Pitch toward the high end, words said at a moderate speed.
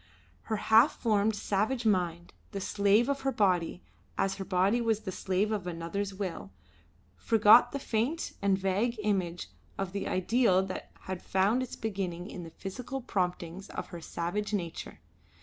Yes: high, 195 Hz; average, 160 wpm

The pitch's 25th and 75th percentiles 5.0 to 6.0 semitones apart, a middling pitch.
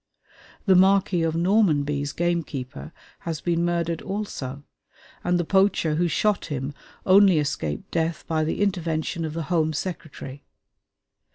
No: average, 3.0 semitones; medium, 165 Hz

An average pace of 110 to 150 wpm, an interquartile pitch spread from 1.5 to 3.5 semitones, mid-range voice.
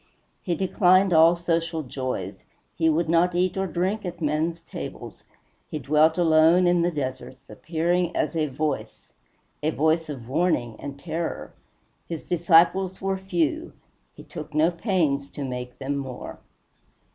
Yes: average, 145 wpm; average, 3.1 semitones; medium, 165 Hz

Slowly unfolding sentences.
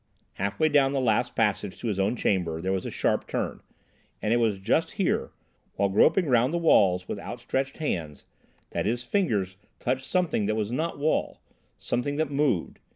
No: average, 180 wpm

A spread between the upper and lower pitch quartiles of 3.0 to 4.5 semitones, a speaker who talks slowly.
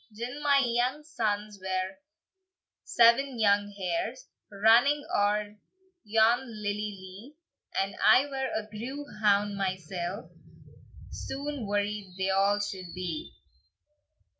Yes: average, 3.6 semitones; slow, 110 wpm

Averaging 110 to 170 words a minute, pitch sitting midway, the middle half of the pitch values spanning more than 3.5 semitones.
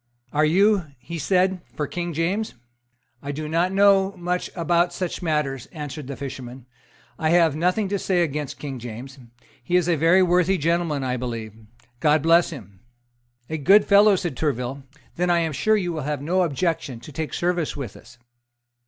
No: average, 180 wpm; medium, 165 Hz; average, 4.2 semitones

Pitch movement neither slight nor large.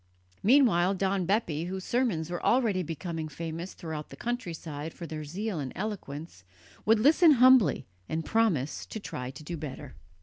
No: wide, 5.8 semitones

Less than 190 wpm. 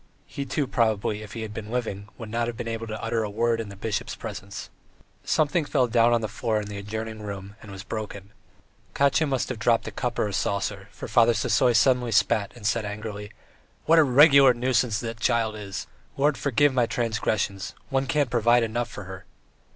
No: fast, 205 wpm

